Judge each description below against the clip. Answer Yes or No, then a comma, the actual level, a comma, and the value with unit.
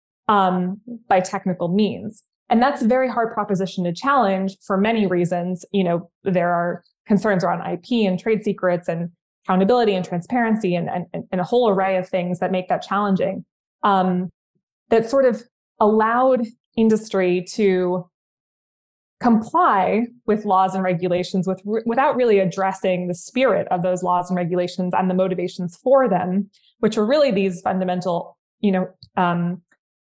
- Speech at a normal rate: Yes, average, 155 wpm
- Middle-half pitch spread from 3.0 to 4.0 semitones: Yes, average, 3.4 semitones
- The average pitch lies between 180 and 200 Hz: Yes, high, 190 Hz